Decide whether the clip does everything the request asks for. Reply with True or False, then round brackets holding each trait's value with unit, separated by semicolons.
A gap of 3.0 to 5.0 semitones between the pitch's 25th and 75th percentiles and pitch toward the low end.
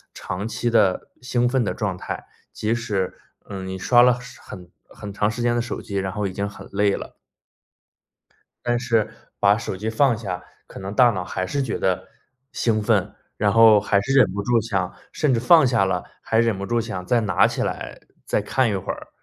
True (3.5 semitones; 110 Hz)